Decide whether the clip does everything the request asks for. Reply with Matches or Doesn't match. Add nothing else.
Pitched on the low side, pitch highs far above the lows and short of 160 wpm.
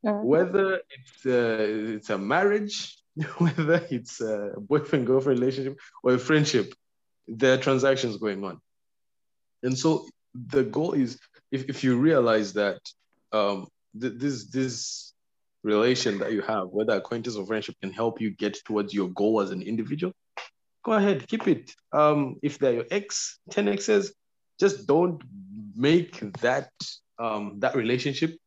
Matches